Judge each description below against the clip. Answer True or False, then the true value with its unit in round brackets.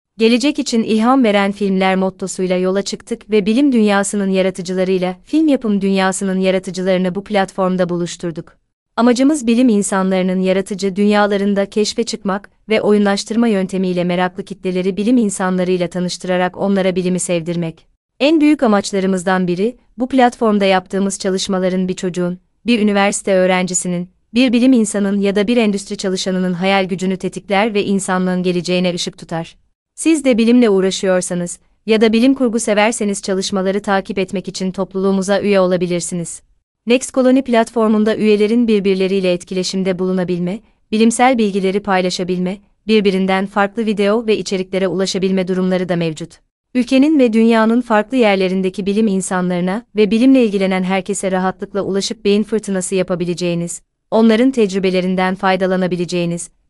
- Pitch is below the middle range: False (195 Hz)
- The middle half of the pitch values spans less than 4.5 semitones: True (2.7 semitones)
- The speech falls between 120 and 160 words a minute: True (125 wpm)